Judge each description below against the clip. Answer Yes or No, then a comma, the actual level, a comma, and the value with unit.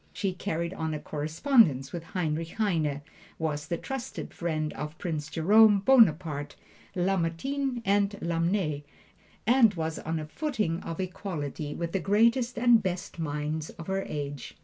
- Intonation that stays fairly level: No, average, 4.8 semitones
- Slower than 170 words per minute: Yes, average, 145 wpm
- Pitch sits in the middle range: Yes, medium, 170 Hz